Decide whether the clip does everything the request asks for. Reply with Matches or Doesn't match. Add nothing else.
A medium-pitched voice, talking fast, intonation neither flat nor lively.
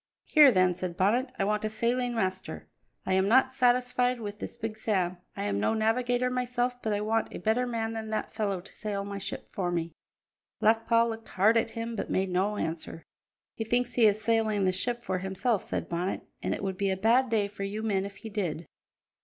Doesn't match